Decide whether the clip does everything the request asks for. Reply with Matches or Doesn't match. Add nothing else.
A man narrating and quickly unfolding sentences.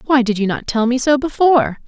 Doesn't match